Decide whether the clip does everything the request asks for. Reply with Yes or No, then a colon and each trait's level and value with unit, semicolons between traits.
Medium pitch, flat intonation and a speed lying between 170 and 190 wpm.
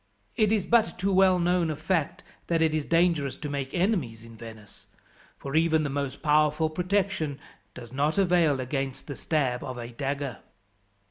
No: medium, 155 Hz; average, 4.5 semitones; average, 175 wpm